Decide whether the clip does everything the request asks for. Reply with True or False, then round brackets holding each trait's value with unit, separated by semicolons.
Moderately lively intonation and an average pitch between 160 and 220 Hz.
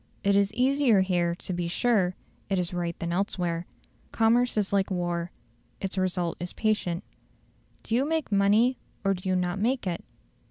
True (3.7 semitones; 190 Hz)